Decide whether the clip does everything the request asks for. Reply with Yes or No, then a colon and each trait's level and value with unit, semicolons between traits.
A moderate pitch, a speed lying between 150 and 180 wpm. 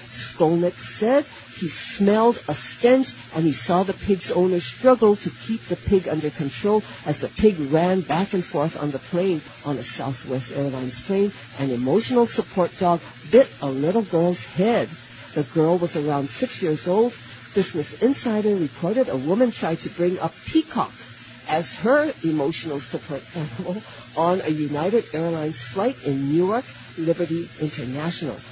Yes: medium, 165 Hz; average, 155 wpm